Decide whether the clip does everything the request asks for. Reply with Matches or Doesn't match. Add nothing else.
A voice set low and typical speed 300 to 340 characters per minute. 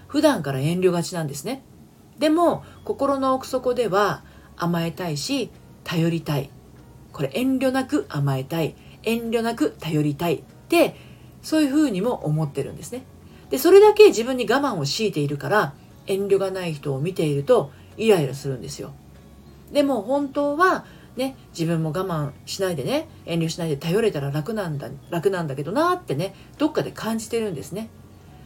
Doesn't match